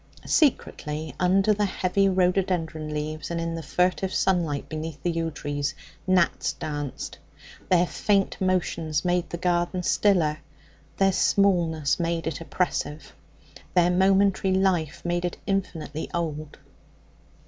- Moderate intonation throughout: Yes, average, 3.1 semitones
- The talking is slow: Yes, slow, 125 wpm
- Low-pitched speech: No, medium, 175 Hz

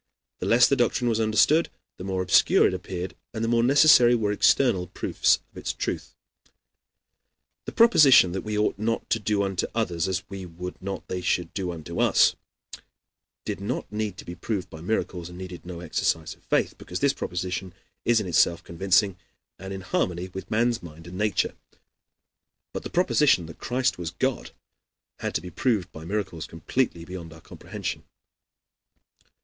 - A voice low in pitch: Yes, very low, 95 Hz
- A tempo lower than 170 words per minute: No, average, 175 wpm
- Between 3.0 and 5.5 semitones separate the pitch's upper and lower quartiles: Yes, average, 4.2 semitones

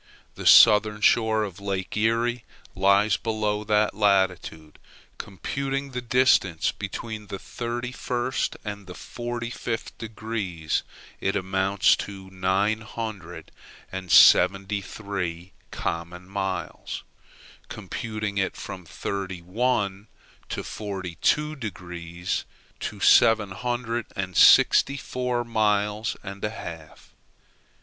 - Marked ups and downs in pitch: No, average, 3.2 semitones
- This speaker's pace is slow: Yes, slow, 110 wpm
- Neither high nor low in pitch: No, low, 105 Hz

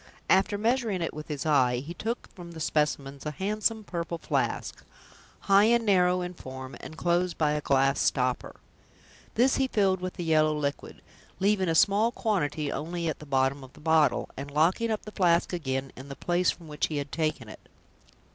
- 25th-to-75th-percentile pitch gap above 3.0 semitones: Yes, average, 5.0 semitones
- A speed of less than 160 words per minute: No, average, 195 wpm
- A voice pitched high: No, medium, 165 Hz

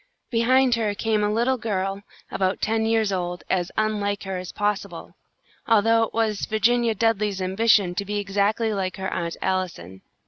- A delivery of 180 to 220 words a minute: No, average, 165 wpm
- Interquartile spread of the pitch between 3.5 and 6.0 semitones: No, average, 2.9 semitones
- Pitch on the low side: No, high, 205 Hz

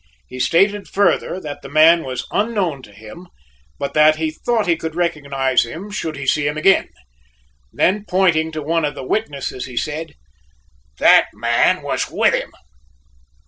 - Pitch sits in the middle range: Yes, medium, 155 Hz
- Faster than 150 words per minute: Yes, average, 165 wpm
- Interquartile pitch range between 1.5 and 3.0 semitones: No, average, 4.2 semitones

